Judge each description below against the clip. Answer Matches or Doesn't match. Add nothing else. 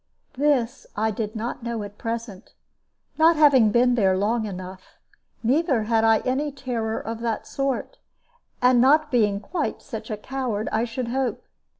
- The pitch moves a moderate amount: Matches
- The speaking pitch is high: Matches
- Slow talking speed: Doesn't match